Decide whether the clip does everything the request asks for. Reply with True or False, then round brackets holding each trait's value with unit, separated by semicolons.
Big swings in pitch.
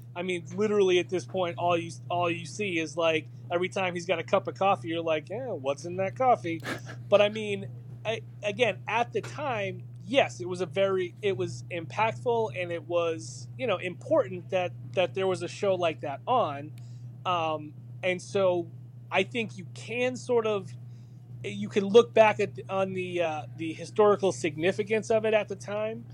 True (7.6 semitones)